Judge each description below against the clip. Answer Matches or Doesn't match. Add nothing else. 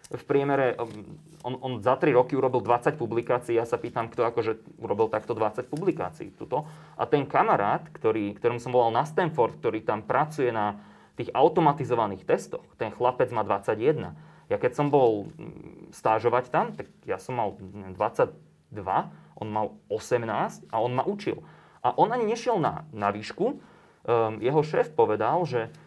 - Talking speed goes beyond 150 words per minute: Matches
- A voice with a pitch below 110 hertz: Doesn't match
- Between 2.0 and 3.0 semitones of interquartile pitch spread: Doesn't match